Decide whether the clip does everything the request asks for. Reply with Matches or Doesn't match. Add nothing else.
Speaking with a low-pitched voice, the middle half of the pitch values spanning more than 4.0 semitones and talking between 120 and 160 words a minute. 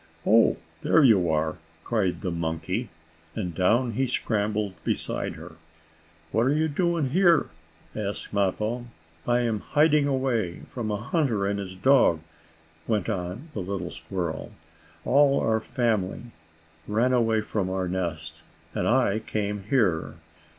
Matches